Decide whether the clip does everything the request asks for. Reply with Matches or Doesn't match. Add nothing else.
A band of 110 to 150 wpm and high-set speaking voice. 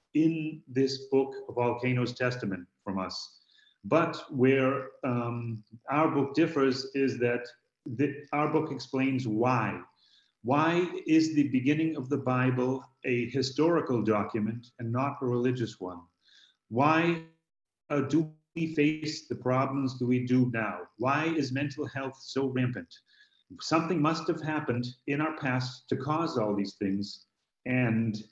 Doesn't match